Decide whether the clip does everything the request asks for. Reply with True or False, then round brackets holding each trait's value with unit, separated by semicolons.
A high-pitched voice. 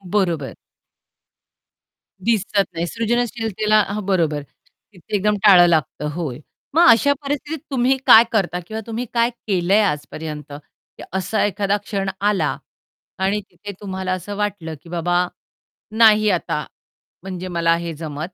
True (195 Hz)